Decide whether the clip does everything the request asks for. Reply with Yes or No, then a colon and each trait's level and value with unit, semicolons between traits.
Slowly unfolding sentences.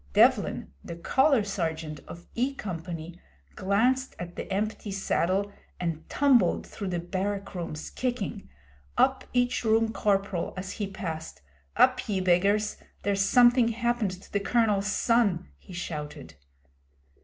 Yes: slow, 130 wpm